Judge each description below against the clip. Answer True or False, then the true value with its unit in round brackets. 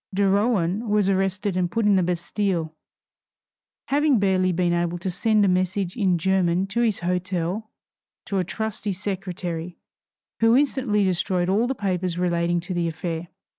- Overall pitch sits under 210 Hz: True (185 Hz)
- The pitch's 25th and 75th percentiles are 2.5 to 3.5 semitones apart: True (2.9 semitones)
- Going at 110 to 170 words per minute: True (160 wpm)